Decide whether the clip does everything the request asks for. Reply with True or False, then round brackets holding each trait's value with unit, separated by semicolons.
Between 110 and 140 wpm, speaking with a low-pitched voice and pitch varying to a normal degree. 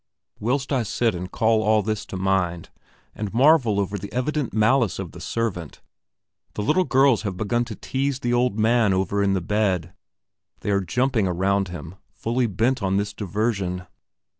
False (175 wpm; 105 Hz; 4.0 semitones)